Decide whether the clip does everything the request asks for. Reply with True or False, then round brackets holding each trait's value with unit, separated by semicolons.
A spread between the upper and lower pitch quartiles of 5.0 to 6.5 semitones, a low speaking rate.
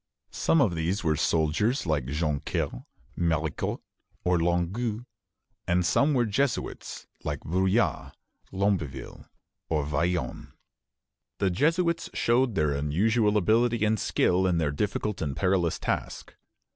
True (5.4 semitones; 120 wpm)